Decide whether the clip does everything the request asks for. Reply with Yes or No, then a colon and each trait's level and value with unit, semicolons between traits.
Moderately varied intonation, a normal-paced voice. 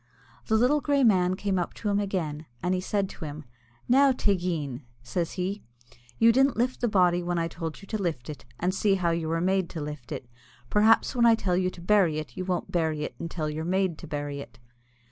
No: average, 4.2 semitones; fast, 225 wpm